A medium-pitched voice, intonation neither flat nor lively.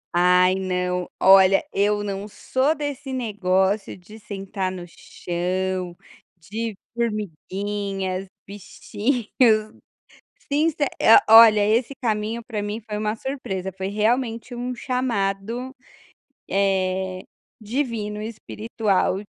No: high, 210 Hz; average, 3.4 semitones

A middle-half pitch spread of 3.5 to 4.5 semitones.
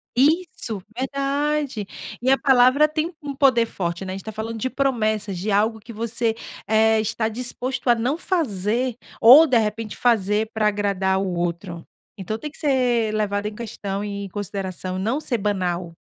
Yes: average, 4.2 semitones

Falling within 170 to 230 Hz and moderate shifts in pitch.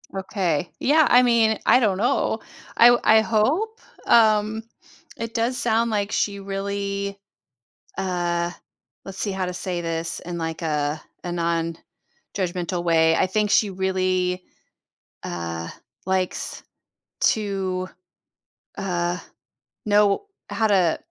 Yes: high, 190 Hz; average, 3.7 semitones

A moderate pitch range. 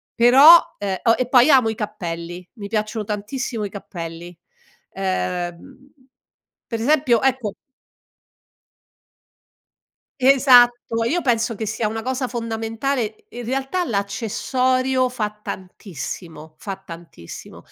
Yes: average, 4.5 semitones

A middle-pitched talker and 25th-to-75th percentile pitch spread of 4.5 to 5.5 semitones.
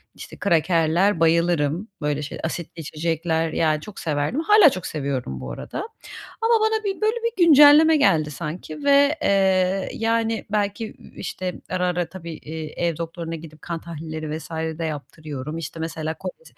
Yes: medium, 170 Hz; average, 4.8 semitones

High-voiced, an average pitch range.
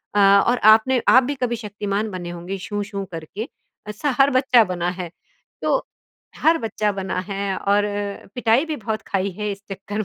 Yes: high, 210 Hz; average, 3.6 semitones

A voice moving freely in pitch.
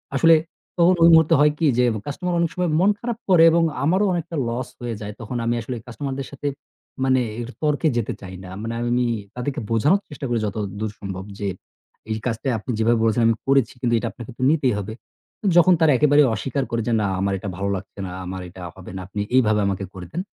Yes: wide, 5.9 semitones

